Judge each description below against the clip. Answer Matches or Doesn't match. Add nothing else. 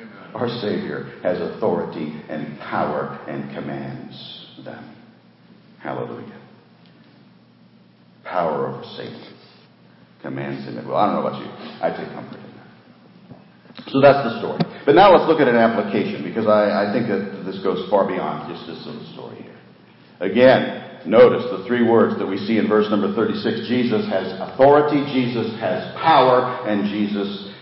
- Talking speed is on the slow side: Doesn't match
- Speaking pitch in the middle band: Doesn't match